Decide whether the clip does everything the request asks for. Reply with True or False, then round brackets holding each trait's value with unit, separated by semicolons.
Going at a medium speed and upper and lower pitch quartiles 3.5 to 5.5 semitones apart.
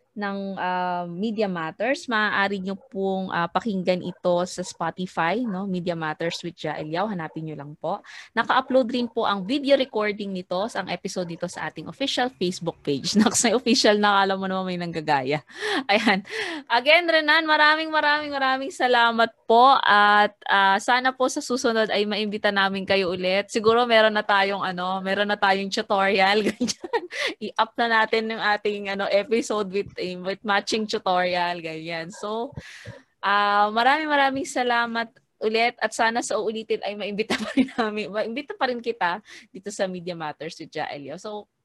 False (160 wpm; 4.2 semitones)